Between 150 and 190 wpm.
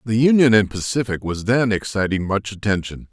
Yes: average, 175 wpm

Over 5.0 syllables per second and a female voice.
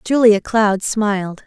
No: 3.7 syllables/s; female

